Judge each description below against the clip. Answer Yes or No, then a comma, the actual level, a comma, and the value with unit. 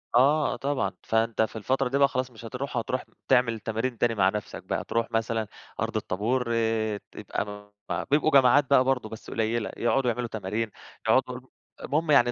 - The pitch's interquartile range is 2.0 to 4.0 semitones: Yes, average, 2.8 semitones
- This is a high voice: No, low, 115 Hz